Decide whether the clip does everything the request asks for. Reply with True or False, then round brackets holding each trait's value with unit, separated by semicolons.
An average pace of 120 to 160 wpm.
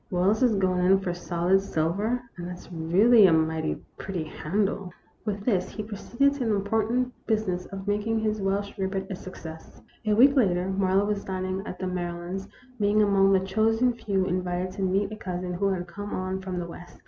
False (195 wpm)